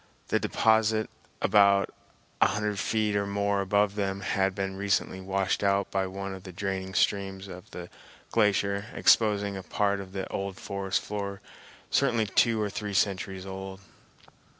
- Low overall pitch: Yes, low, 100 Hz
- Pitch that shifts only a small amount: Yes, narrow, 1.1 semitones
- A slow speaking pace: No, average, 155 wpm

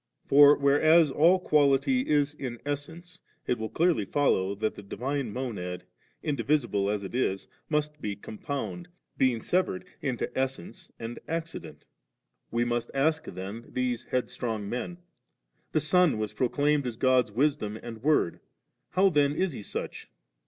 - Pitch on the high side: No, low, 135 Hz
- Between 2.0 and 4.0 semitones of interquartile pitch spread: No, average, 4.9 semitones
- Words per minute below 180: Yes, average, 145 wpm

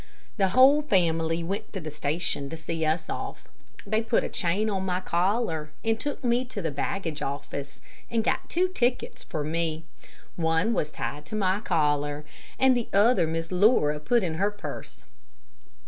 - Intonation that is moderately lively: No, wide, 5.7 semitones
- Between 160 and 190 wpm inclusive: Yes, average, 175 wpm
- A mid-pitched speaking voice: Yes, medium, 180 Hz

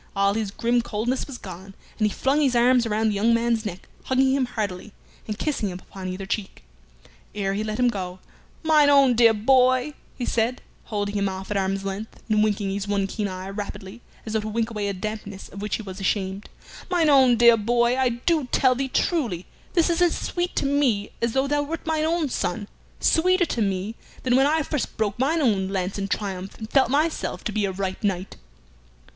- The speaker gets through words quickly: Yes, fast, 215 wpm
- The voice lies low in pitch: No, high, 220 Hz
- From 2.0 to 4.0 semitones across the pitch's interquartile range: No, average, 4.9 semitones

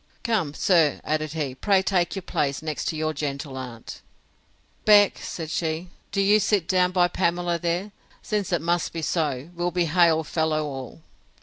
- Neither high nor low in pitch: Yes, medium, 170 Hz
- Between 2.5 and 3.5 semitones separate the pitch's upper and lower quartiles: Yes, average, 2.9 semitones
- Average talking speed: Yes, average, 165 wpm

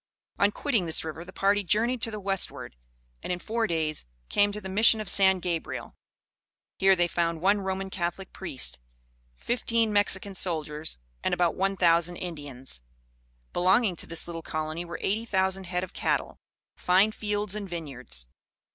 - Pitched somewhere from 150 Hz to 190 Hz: Yes, medium, 185 Hz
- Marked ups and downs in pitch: No, average, 3.5 semitones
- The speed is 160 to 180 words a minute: Yes, average, 165 wpm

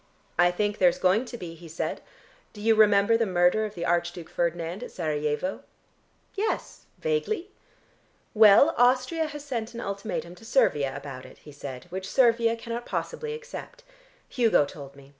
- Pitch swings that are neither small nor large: No, wide, 6.0 semitones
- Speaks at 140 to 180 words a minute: Yes, average, 160 wpm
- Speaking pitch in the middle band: No, high, 205 Hz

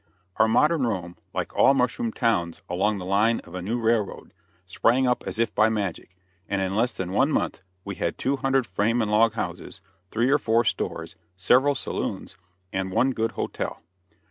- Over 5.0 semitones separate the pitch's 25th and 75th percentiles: No, average, 4.5 semitones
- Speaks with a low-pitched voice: Yes, low, 110 Hz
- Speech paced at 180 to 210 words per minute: Yes, average, 185 wpm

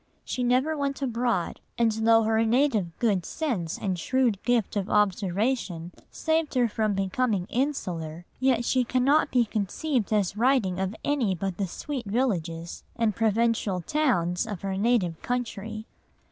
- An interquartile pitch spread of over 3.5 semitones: Yes, average, 4.7 semitones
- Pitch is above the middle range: Yes, high, 225 Hz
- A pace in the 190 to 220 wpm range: No, average, 150 wpm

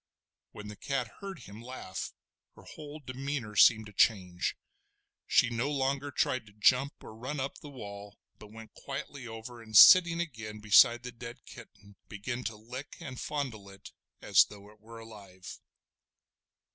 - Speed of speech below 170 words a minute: Yes, average, 160 wpm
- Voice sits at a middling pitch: No, low, 115 Hz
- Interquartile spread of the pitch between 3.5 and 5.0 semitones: Yes, average, 4.1 semitones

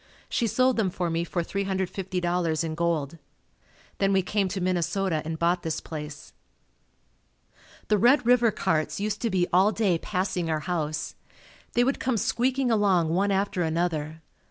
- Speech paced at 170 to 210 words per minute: No, average, 155 wpm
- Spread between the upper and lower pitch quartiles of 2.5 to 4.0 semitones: Yes, average, 3.7 semitones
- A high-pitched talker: No, medium, 180 Hz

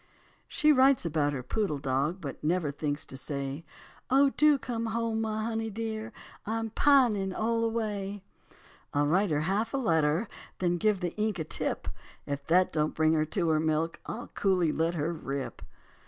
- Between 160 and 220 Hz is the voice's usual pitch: Yes, medium, 185 Hz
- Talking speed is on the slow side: No, average, 175 wpm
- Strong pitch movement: Yes, wide, 6.4 semitones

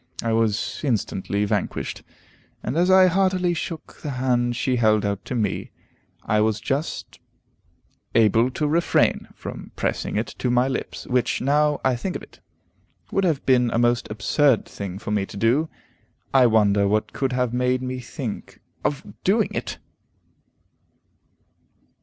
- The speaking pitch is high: No, low, 125 Hz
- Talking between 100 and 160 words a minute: Yes, average, 155 wpm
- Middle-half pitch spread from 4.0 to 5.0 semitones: Yes, average, 4.7 semitones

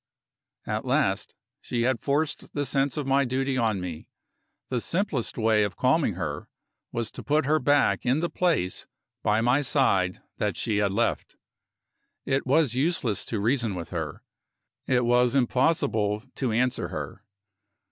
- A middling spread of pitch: Yes, average, 4.6 semitones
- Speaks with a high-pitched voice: No, low, 125 Hz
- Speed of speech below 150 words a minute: No, average, 155 wpm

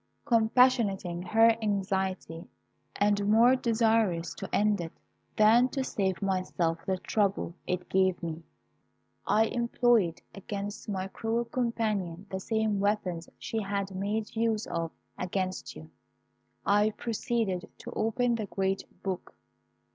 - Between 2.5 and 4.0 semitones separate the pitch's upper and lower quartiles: Yes, average, 3.1 semitones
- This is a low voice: No, high, 205 Hz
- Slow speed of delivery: Yes, slow, 125 wpm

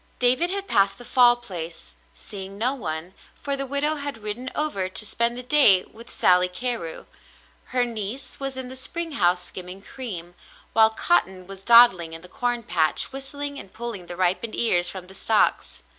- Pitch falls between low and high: No, high, 225 Hz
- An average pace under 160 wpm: No, average, 180 wpm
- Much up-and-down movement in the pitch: Yes, wide, 5.9 semitones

